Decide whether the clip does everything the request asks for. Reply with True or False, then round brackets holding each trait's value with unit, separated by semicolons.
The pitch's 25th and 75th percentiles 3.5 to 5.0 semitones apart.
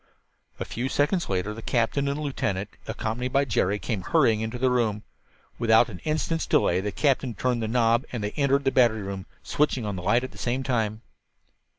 True (3.8 semitones)